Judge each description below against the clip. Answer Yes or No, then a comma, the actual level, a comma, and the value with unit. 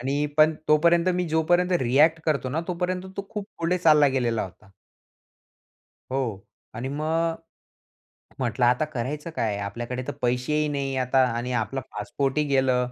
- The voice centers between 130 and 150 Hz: Yes, medium, 140 Hz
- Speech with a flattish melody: No, average, 4.4 semitones